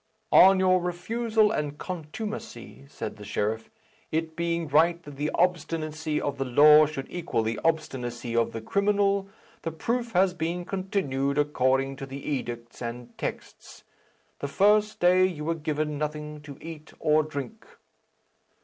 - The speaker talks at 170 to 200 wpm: No, average, 150 wpm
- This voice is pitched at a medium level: Yes, medium, 155 Hz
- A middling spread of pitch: Yes, average, 4.6 semitones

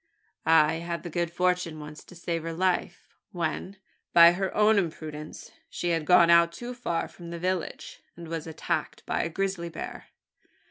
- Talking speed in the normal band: Yes, average, 175 wpm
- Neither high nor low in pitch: Yes, medium, 170 Hz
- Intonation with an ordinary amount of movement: No, narrow, 1.8 semitones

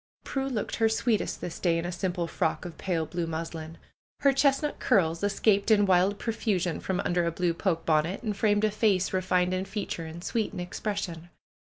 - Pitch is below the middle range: No, medium, 185 Hz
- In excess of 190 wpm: Yes, average, 200 wpm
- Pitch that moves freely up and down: No, average, 3.8 semitones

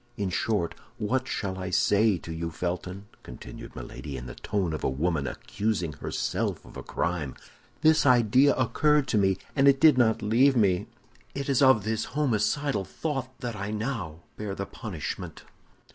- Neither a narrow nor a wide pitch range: No, wide, 6.4 semitones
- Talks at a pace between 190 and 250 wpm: No, average, 165 wpm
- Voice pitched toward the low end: Yes, low, 105 Hz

